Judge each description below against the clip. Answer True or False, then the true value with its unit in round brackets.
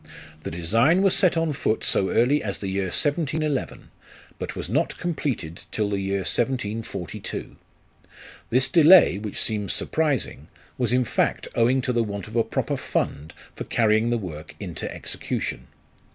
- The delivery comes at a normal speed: True (155 wpm)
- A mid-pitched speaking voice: False (115 Hz)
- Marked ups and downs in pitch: True (6.1 semitones)